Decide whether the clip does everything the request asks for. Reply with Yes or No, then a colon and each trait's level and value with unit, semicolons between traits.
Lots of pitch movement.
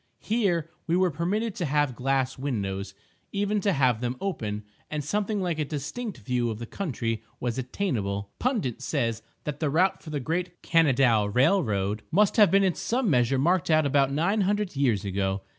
Yes: wide, 7.9 semitones